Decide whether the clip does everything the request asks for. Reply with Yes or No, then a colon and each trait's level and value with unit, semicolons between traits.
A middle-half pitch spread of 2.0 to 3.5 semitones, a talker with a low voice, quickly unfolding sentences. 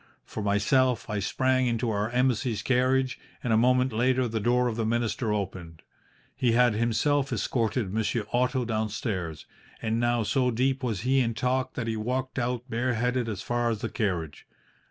No: average, 2.7 semitones; low, 120 Hz; average, 175 wpm